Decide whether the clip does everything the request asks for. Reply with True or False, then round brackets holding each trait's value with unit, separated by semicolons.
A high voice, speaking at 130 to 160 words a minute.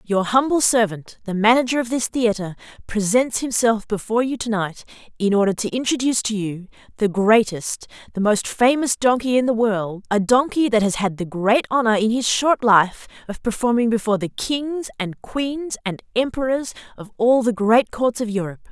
False (225 Hz; 180 wpm)